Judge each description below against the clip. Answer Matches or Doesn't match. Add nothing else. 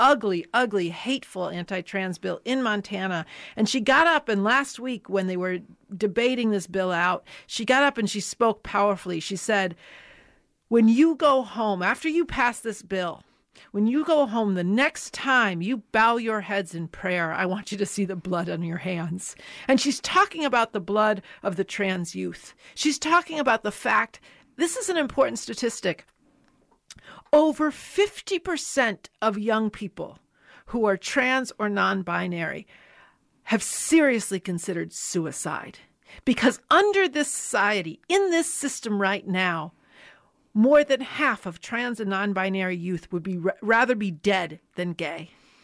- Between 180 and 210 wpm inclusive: Doesn't match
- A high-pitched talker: Matches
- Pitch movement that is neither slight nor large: Doesn't match